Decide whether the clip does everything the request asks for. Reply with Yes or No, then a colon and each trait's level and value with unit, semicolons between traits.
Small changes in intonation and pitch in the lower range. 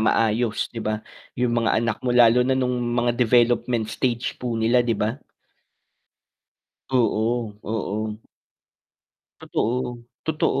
Yes: narrow, 1.7 semitones; low, 120 Hz